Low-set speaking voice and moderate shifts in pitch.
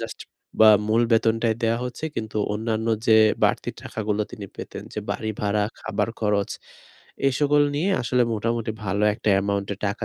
No: low, 110 Hz; narrow, 1.9 semitones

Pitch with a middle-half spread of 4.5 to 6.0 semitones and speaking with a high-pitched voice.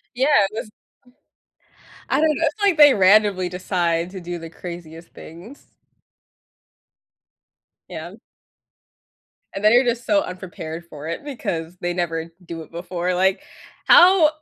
No: wide, 5.6 semitones; medium, 180 Hz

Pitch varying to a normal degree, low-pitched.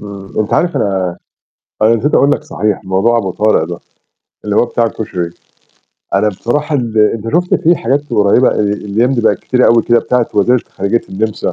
Yes: average, 3.1 semitones; low, 110 Hz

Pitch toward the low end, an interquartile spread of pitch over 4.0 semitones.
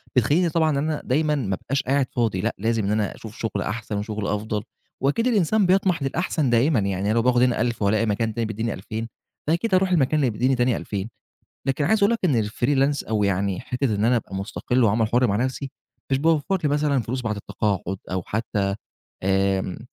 Yes: low, 120 Hz; average, 5.3 semitones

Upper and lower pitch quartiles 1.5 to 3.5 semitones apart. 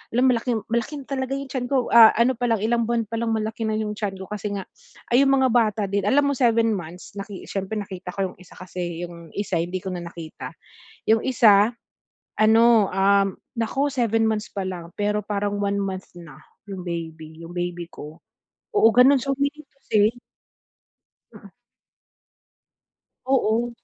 No: average, 4.0 semitones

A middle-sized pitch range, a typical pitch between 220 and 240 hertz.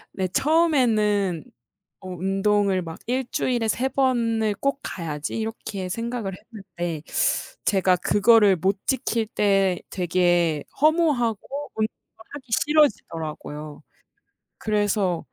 No: average, 4.7 semitones; high, 205 Hz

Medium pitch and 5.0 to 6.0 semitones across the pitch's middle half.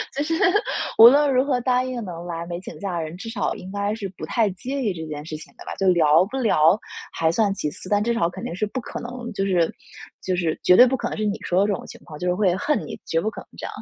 No: high, 200 Hz; wide, 5.5 semitones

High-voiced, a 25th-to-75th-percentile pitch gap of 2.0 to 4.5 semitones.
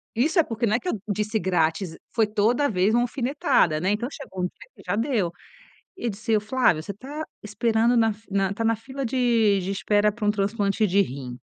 Yes: high, 215 Hz; average, 3.3 semitones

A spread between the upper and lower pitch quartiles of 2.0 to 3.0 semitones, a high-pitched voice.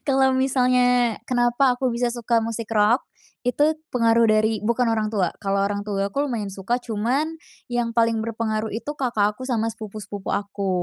Yes: average, 2.7 semitones; high, 230 Hz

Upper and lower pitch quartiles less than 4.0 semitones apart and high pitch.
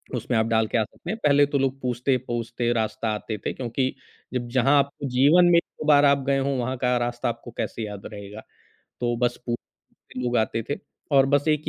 No: average, 3.1 semitones; low, 125 Hz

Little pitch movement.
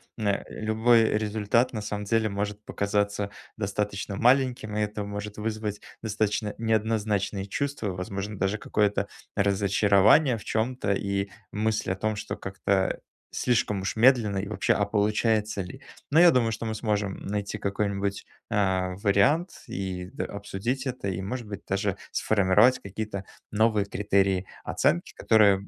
Yes: narrow, 1.9 semitones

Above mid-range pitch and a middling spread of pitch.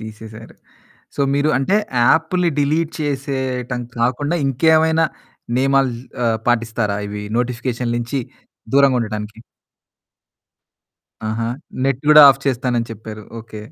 No: low, 125 Hz; average, 3.7 semitones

